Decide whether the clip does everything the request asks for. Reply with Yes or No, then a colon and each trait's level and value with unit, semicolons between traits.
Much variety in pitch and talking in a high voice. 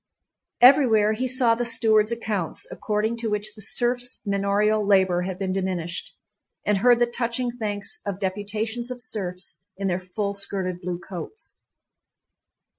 No: average, 3.5 semitones; high, 210 Hz